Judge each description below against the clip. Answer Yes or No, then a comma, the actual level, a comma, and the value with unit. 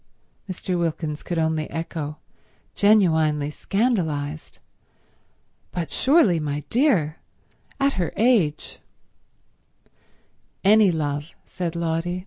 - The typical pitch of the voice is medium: Yes, medium, 165 Hz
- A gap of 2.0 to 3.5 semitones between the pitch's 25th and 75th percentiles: No, average, 4.4 semitones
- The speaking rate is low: Yes, slow, 90 wpm